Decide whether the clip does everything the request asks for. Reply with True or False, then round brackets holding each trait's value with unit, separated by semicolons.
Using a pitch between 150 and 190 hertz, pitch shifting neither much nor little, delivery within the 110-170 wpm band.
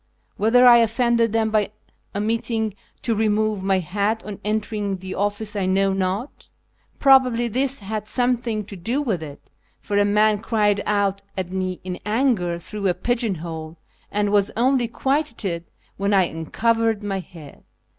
False (210 Hz; 3.1 semitones; 155 wpm)